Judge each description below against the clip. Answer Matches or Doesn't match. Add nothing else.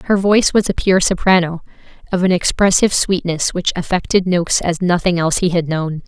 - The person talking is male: Doesn't match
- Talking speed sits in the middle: Matches